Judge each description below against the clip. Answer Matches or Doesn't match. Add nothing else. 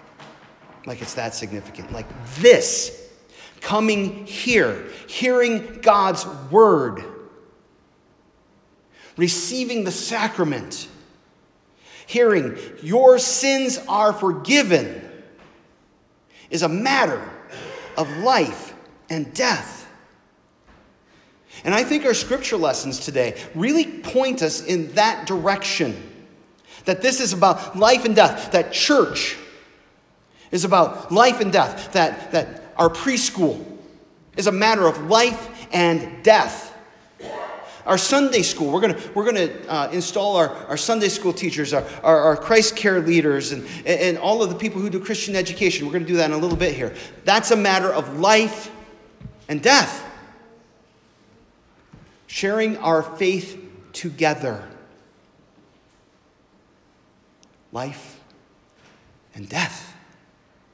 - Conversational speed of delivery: Doesn't match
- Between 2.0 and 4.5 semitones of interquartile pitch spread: Doesn't match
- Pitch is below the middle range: Doesn't match